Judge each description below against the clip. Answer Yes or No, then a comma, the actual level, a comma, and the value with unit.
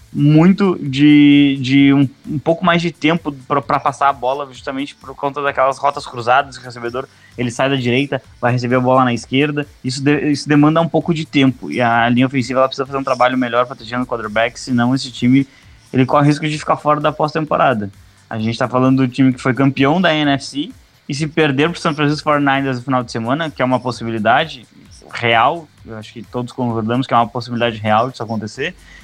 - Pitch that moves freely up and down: No, average, 3.0 semitones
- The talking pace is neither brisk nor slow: No, fast, 215 wpm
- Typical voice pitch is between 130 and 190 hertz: Yes, low, 135 Hz